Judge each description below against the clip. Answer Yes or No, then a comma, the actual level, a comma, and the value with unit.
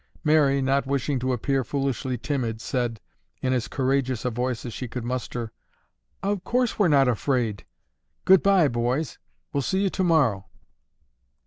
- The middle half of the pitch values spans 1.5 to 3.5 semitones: Yes, average, 3.2 semitones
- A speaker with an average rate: Yes, average, 145 wpm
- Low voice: Yes, low, 130 Hz